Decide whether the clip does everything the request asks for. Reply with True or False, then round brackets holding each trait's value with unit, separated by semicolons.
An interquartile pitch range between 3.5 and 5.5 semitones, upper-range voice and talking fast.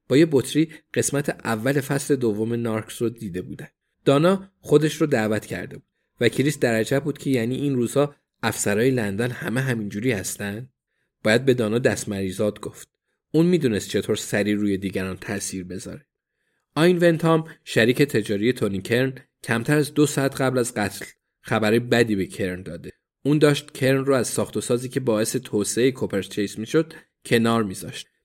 False (4.8 semitones; 120 Hz; 160 wpm)